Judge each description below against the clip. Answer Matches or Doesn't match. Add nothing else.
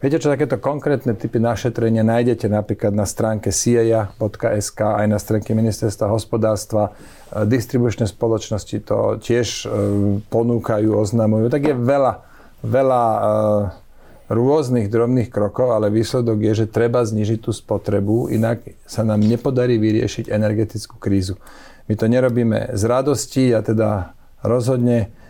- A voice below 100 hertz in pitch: Doesn't match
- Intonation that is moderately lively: Doesn't match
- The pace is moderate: Matches